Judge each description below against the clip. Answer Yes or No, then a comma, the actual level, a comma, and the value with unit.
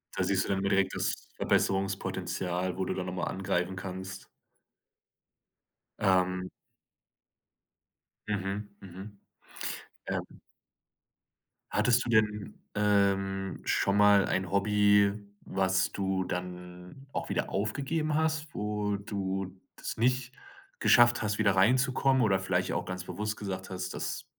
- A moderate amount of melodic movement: No, narrow, 2.0 semitones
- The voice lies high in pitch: No, low, 100 Hz